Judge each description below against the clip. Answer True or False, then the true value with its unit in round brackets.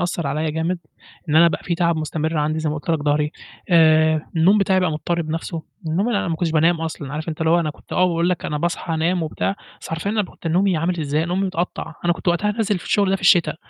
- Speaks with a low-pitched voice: False (165 Hz)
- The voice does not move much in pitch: True (2.3 semitones)